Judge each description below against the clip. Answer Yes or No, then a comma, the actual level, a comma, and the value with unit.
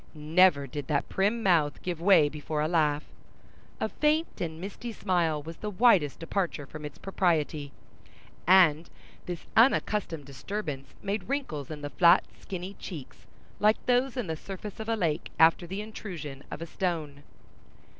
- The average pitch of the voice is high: No, medium, 170 Hz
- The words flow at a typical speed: Yes, average, 155 wpm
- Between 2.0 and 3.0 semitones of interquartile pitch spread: No, average, 5.0 semitones